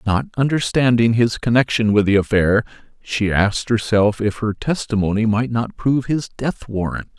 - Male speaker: Yes, male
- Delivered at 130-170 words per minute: Yes, average, 160 wpm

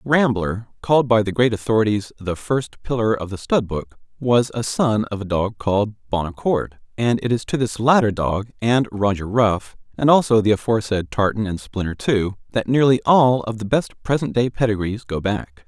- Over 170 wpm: Yes, average, 190 wpm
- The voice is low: Yes, low, 110 Hz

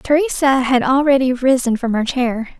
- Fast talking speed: No, average, 160 wpm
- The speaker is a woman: Yes, female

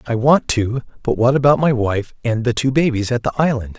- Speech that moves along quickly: Yes, fast, 240 wpm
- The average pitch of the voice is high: No, low, 125 Hz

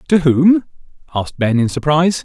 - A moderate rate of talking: Yes, average, 160 wpm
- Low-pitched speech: No, medium, 155 Hz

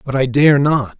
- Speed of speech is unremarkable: No, fast, 240 wpm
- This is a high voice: No, low, 135 Hz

